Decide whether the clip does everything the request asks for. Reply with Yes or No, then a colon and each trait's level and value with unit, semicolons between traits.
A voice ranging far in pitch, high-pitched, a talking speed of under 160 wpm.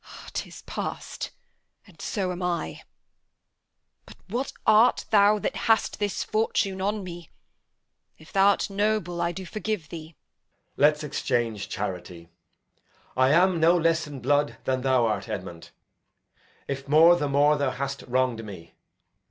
No: wide, 6.7 semitones; medium, 155 Hz; average, 140 wpm